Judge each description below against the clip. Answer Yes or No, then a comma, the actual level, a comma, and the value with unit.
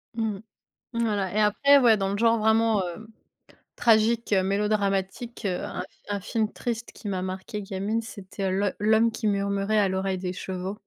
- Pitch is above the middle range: Yes, high, 205 Hz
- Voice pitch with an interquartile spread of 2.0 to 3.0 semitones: Yes, narrow, 2.4 semitones